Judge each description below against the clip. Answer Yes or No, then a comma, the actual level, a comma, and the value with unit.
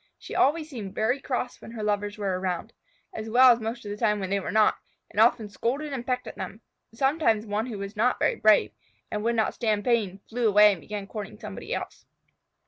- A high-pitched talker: Yes, high, 220 Hz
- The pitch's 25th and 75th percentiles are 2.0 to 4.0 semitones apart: Yes, average, 2.8 semitones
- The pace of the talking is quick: Yes, fast, 220 wpm